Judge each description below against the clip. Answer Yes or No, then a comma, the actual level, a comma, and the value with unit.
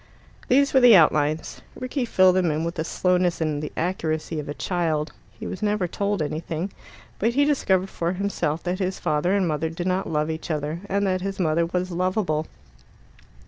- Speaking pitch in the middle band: Yes, medium, 175 Hz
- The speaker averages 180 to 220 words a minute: Yes, average, 190 wpm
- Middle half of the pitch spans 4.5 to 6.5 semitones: No, average, 3.4 semitones